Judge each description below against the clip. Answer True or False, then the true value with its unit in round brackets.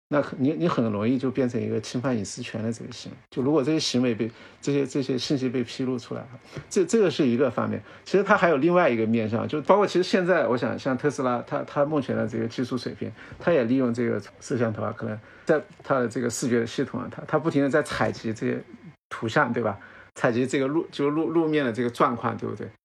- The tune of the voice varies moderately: True (4.0 semitones)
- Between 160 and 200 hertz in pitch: False (125 Hz)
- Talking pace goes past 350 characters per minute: True (360 characters per minute)